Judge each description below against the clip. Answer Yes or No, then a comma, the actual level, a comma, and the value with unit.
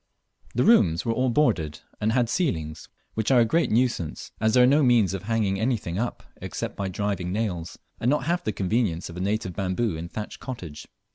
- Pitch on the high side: No, low, 110 Hz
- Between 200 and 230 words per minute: Yes, fast, 205 wpm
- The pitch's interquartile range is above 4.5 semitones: Yes, average, 5.2 semitones